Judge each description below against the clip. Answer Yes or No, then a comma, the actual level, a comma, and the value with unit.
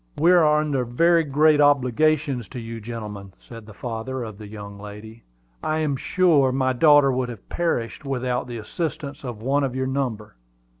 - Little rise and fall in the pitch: No, average, 4.4 semitones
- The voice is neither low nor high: No, low, 130 Hz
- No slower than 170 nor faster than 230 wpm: Yes, average, 185 wpm